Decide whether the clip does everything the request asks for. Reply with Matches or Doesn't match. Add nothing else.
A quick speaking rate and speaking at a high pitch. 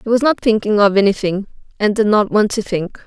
Matches